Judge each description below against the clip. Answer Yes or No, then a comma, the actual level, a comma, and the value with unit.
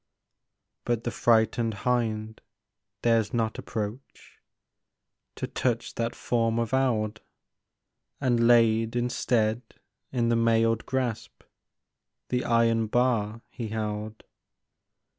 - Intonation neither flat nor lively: No, narrow, 1.4 semitones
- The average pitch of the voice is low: Yes, low, 115 Hz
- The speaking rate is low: Yes, slow, 100 wpm